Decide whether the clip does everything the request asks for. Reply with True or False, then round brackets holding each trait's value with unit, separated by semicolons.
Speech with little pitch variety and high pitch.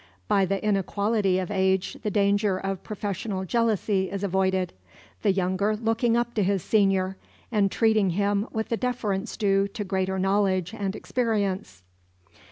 True (2.1 semitones; 200 Hz)